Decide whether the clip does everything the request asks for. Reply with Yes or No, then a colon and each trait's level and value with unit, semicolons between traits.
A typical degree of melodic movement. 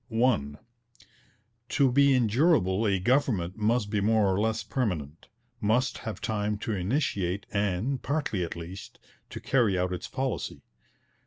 Yes: average, 5.0 semitones